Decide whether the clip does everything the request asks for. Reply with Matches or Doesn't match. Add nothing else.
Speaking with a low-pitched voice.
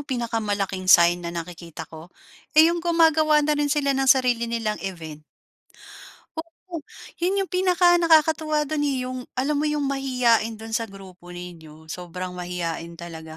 Doesn't match